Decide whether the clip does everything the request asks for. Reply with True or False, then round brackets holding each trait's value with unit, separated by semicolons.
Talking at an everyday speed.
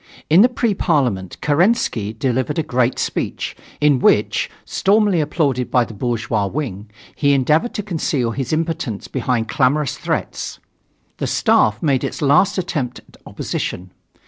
True (145 wpm)